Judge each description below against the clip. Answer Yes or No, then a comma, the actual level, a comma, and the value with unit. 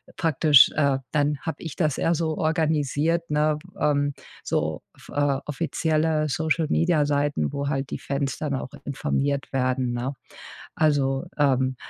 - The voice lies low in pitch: No, medium, 145 Hz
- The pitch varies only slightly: Yes, narrow, 2.3 semitones